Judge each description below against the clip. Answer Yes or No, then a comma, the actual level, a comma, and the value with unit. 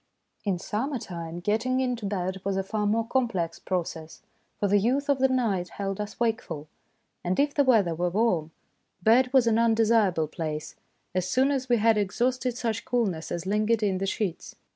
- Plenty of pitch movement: No, average, 4.6 semitones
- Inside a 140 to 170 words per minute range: No, average, 185 wpm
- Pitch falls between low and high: No, high, 210 Hz